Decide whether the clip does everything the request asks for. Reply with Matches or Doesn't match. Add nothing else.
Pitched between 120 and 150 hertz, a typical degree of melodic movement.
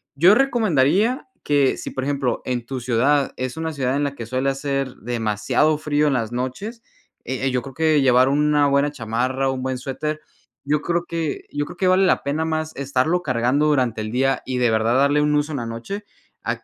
Matches